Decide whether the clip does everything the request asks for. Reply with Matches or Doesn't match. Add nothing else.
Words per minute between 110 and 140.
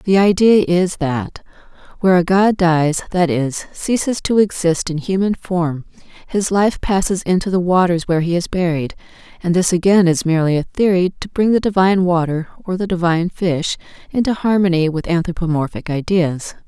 Doesn't match